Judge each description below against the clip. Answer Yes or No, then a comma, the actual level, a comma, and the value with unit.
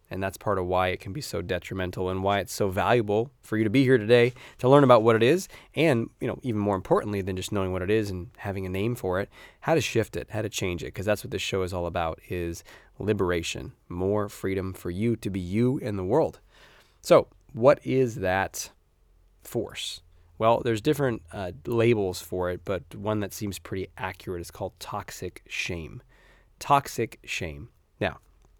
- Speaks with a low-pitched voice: Yes, low, 100 Hz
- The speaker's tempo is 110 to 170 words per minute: No, fast, 205 wpm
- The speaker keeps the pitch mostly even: No, average, 3.7 semitones